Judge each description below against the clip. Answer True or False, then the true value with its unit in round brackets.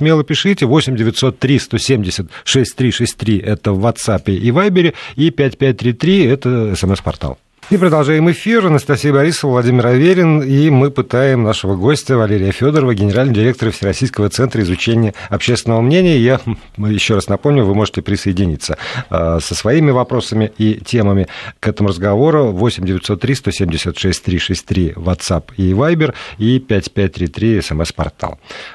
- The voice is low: True (115 Hz)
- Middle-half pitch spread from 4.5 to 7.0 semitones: True (5.5 semitones)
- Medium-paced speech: True (135 wpm)